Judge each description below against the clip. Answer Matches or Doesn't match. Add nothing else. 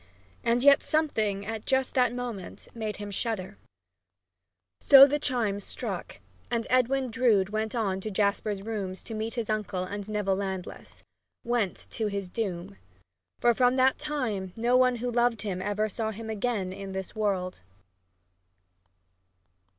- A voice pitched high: Matches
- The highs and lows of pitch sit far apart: Doesn't match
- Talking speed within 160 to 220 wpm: Doesn't match